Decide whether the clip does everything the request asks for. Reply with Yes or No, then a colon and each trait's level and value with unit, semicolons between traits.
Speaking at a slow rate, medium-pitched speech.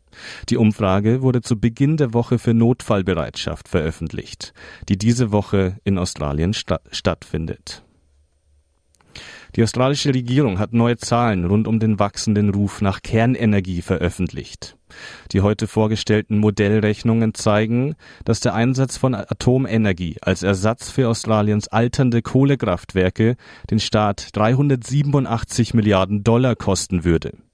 No: slow, 115 wpm; low, 110 Hz